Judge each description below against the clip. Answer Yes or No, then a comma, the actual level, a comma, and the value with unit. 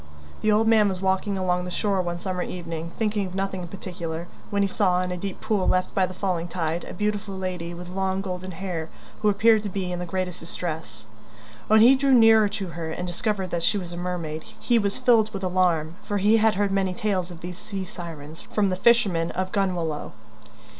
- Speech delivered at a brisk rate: Yes, fast, 220 wpm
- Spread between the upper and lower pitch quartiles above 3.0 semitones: No, average, 2.7 semitones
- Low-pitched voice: No, medium, 185 Hz